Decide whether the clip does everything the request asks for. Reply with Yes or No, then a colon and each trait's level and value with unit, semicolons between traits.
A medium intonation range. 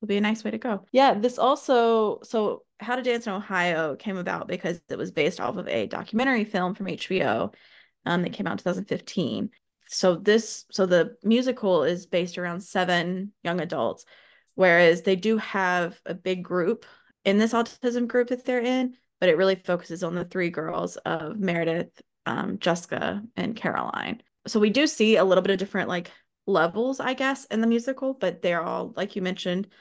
Yes: average, 4.6 semitones